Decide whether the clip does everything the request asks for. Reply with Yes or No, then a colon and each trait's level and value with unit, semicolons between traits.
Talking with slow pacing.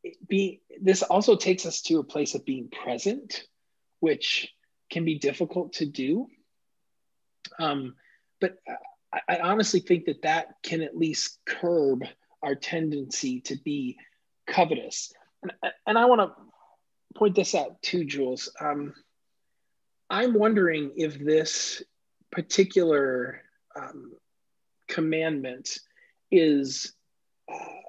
Yes: slow, 115 wpm